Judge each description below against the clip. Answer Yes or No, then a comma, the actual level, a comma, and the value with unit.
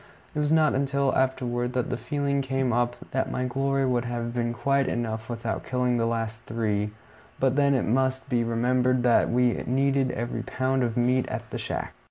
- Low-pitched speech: Yes, low, 125 Hz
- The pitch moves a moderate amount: No, narrow, 2.0 semitones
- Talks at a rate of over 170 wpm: Yes, average, 195 wpm